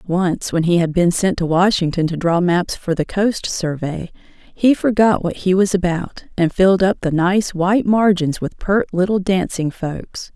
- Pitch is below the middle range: No, medium, 180 Hz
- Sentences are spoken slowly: No, average, 190 wpm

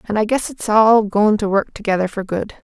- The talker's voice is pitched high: Yes, high, 210 Hz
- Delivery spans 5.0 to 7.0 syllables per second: Yes, 5.3 syllables/s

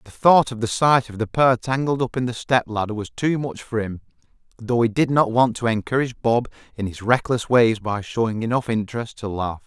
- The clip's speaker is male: Yes, male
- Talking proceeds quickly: Yes, fast, 230 wpm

